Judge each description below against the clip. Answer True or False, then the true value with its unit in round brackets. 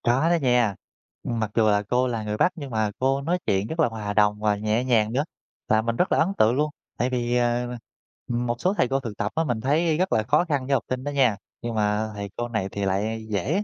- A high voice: False (120 Hz)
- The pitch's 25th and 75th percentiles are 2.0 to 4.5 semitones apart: True (3.9 semitones)